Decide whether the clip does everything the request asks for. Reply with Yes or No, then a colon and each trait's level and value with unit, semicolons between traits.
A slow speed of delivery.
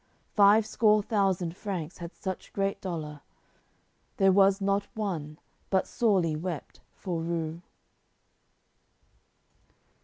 Yes: slow, 100 wpm